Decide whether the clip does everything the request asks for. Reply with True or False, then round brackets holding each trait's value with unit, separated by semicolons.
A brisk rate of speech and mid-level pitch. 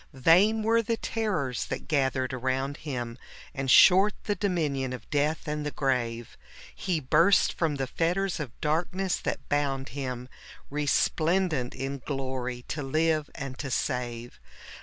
False (145 wpm; 145 Hz)